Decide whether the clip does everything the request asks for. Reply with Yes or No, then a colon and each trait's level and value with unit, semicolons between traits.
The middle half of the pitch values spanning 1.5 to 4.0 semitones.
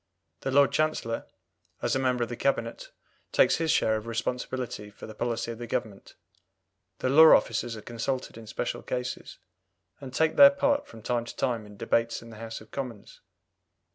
Yes: average, 3.0 semitones